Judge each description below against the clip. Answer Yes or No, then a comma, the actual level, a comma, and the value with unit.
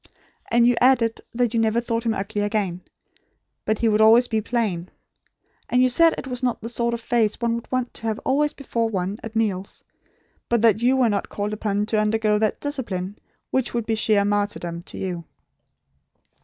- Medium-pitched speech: No, high, 225 Hz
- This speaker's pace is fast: No, average, 195 wpm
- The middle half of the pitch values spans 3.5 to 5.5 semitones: No, narrow, 2.5 semitones